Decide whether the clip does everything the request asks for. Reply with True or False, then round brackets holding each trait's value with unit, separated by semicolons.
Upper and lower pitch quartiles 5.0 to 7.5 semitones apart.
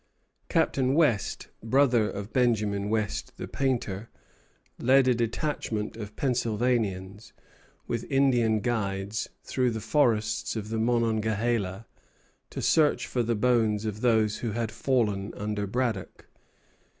False (2.8 semitones)